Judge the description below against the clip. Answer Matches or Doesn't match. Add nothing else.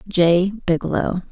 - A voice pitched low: Doesn't match